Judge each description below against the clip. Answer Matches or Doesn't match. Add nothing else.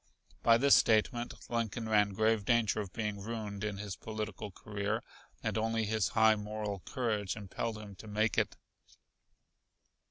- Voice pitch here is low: Matches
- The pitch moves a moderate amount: Doesn't match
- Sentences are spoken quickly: Doesn't match